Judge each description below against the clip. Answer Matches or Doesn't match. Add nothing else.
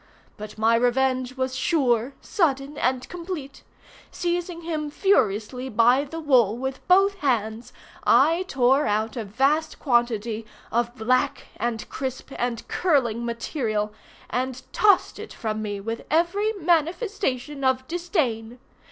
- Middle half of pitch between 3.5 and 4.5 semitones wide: Doesn't match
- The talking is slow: Matches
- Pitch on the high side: Matches